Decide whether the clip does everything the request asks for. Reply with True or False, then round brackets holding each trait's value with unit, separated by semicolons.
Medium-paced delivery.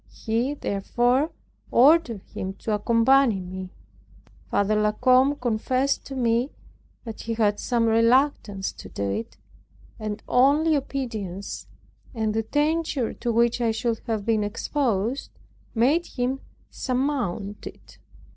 False (125 wpm)